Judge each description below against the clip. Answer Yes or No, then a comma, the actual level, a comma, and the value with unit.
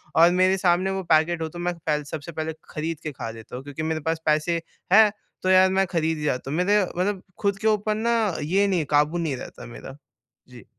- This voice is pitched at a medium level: Yes, medium, 165 Hz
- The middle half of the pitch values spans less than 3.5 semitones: No, average, 3.8 semitones